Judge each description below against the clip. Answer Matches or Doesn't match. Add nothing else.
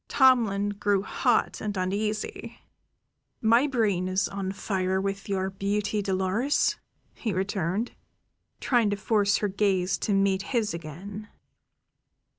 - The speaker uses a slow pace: Matches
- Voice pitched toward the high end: Matches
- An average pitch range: Doesn't match